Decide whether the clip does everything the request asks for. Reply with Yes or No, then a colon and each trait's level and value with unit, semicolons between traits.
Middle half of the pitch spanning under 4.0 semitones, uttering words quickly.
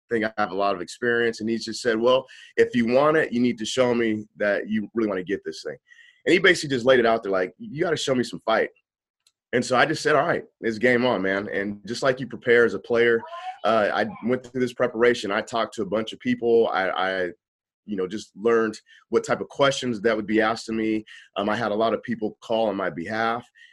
Yes: average, 2.9 semitones; fast, 265 wpm